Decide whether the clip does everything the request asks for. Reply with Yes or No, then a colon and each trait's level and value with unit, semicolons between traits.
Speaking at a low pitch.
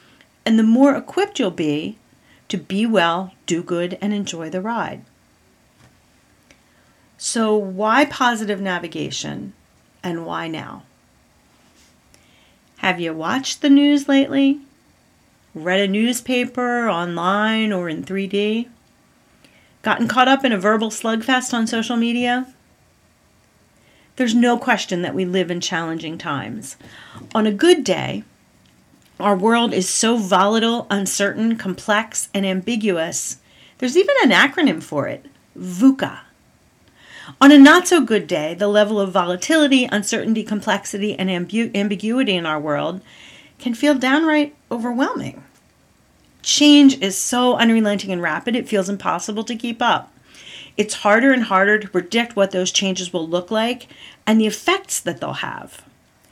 No: high, 215 Hz